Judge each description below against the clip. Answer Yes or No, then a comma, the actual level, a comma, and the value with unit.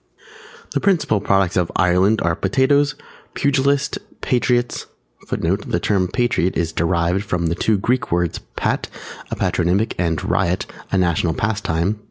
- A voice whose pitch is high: No, very low, 95 Hz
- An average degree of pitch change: No, wide, 5.7 semitones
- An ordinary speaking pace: Yes, average, 155 wpm